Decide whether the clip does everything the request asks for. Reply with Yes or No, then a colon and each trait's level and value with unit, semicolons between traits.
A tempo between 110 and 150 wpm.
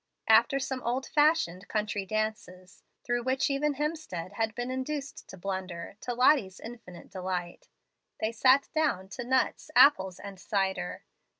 Yes: average, 140 wpm